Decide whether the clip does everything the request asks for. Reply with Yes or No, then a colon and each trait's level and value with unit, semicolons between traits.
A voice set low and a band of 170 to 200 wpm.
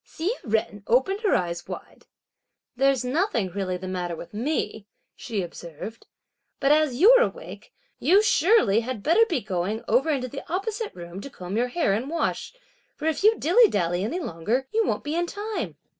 No: very high, 250 Hz; average, 180 wpm